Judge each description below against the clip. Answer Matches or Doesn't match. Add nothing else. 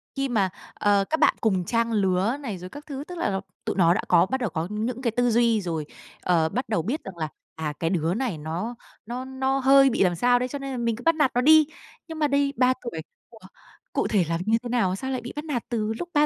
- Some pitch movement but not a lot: Doesn't match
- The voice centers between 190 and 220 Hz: Doesn't match